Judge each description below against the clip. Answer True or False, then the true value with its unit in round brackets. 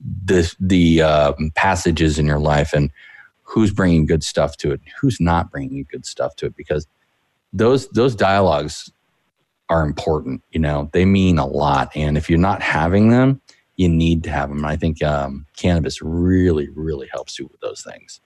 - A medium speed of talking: True (185 wpm)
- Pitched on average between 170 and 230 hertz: False (85 Hz)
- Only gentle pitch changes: False (3.9 semitones)